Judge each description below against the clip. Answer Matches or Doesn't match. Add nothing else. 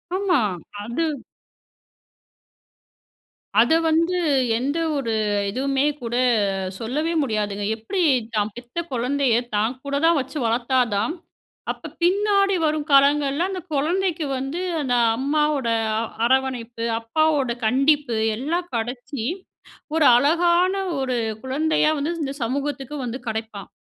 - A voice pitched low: Doesn't match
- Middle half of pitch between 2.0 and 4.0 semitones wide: Doesn't match